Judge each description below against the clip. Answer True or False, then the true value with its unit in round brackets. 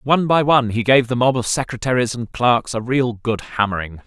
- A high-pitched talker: False (120 Hz)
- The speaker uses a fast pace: True (220 wpm)